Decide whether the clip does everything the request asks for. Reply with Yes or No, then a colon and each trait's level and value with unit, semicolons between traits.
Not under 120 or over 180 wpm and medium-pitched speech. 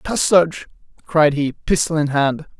Yes: average, 140 wpm; medium, 155 Hz